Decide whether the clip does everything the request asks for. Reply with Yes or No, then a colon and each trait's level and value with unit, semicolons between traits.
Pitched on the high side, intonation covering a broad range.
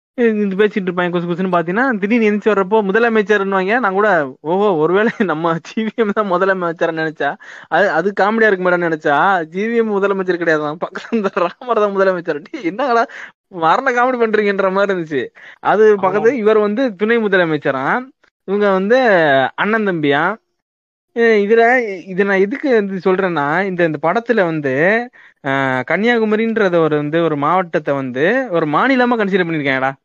No: high, 200 Hz; average, 4.6 semitones